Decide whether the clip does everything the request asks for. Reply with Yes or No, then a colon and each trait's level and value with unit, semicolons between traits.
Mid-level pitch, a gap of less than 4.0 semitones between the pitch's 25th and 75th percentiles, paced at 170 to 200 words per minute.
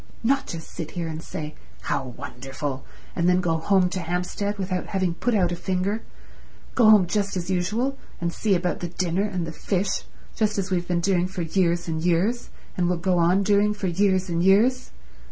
Yes: medium, 180 Hz; average, 2.7 semitones; average, 195 wpm